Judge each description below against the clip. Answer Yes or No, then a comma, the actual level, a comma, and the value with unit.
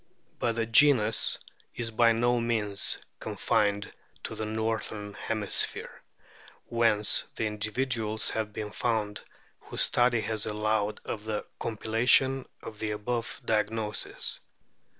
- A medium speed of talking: No, slow, 115 wpm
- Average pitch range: No, narrow, 1.7 semitones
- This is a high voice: No, low, 110 Hz